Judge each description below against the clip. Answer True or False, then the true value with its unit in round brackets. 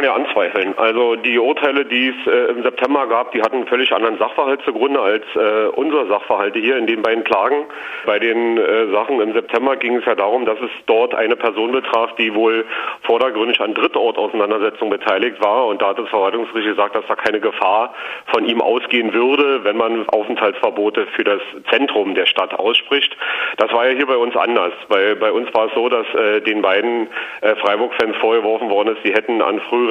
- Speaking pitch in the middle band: False (120 Hz)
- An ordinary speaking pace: False (200 wpm)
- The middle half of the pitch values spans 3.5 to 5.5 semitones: True (3.8 semitones)